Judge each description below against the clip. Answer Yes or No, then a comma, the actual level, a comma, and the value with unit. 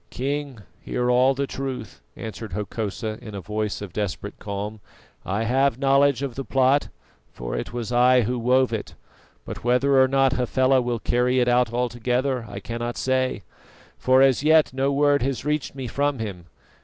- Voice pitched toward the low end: Yes, low, 125 Hz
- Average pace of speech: Yes, average, 175 wpm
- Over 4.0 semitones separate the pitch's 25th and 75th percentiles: No, average, 3.1 semitones